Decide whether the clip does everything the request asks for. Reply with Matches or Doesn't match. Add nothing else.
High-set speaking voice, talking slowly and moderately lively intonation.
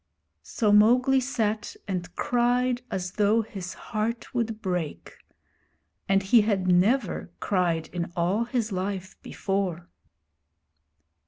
Matches